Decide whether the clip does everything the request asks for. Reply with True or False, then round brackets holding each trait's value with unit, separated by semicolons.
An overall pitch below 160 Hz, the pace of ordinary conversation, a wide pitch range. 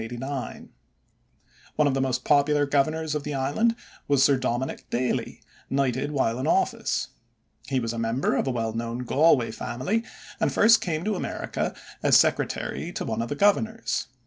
False (135 Hz; 165 wpm; 3.7 semitones)